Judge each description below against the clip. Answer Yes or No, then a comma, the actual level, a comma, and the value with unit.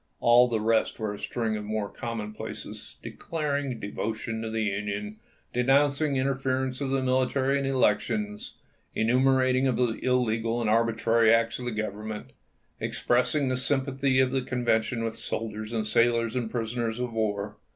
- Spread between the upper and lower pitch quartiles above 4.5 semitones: No, average, 2.9 semitones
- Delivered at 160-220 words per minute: No, average, 150 wpm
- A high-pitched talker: No, low, 115 Hz